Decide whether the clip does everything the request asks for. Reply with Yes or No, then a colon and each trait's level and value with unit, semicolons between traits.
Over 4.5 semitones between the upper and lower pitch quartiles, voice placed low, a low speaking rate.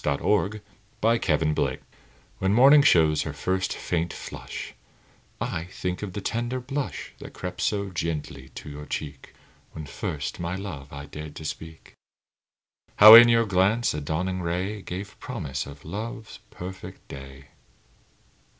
No: wide, 5.5 semitones; very low, 90 Hz; average, 145 wpm